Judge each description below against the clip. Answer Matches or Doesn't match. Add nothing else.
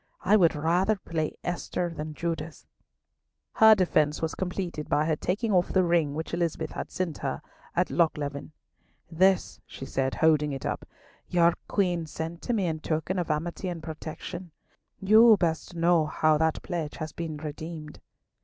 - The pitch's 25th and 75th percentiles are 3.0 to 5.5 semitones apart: Doesn't match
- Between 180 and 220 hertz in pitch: Doesn't match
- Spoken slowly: Doesn't match